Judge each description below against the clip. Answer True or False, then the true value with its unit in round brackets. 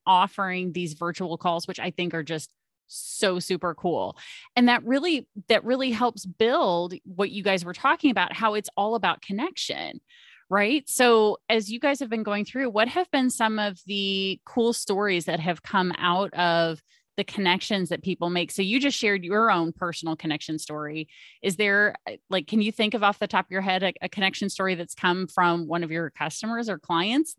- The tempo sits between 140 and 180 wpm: False (200 wpm)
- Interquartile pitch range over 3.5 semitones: True (4.1 semitones)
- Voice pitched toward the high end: True (195 Hz)